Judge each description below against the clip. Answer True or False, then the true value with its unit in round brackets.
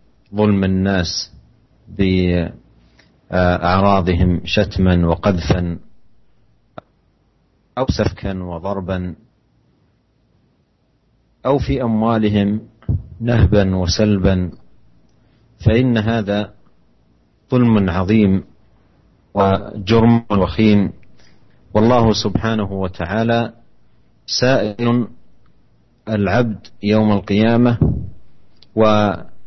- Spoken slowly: True (55 wpm)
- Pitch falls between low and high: False (100 Hz)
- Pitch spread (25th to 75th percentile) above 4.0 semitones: False (3.4 semitones)